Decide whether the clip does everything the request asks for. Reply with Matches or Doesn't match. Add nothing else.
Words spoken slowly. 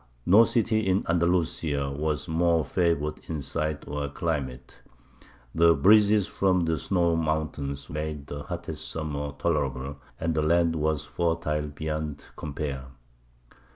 Matches